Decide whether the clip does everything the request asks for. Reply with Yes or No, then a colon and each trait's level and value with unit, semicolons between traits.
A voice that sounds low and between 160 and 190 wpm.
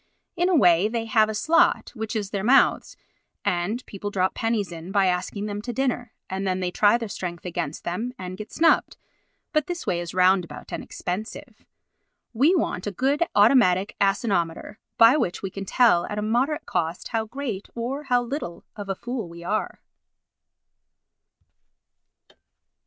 No: high, 210 Hz; average, 170 wpm